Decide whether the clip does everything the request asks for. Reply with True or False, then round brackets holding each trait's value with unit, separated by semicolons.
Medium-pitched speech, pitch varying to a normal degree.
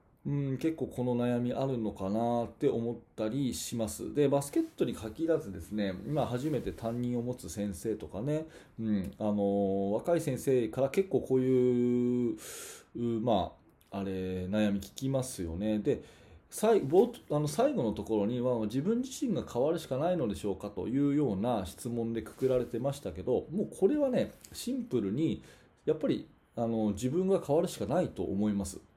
False (120 Hz; 5.0 semitones)